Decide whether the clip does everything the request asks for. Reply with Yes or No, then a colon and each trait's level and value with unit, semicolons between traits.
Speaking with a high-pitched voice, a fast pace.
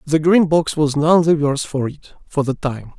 No: medium, 150 Hz; fast, 240 wpm